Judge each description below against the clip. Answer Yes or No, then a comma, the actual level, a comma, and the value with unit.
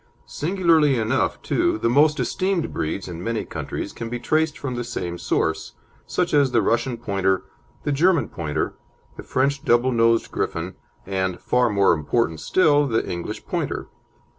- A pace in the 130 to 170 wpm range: Yes, average, 160 wpm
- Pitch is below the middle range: Yes, low, 120 Hz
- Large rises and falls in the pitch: Yes, wide, 6.9 semitones